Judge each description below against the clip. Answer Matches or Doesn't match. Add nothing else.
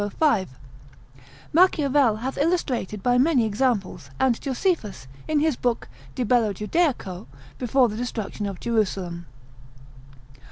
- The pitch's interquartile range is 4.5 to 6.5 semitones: Matches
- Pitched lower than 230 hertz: Doesn't match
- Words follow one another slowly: Matches